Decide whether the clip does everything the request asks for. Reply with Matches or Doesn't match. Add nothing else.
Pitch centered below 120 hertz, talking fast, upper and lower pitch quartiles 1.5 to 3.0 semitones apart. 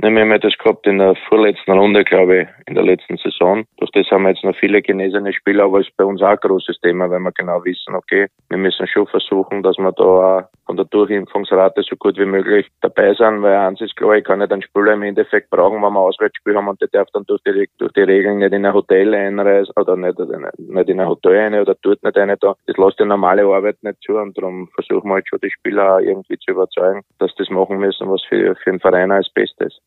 Matches